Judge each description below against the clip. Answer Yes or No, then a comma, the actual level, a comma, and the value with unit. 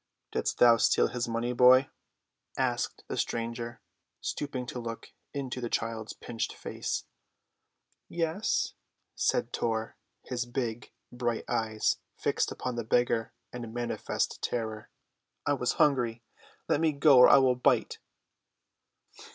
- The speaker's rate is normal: No, slow, 125 wpm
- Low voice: Yes, low, 120 Hz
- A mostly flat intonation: Yes, narrow, 1.8 semitones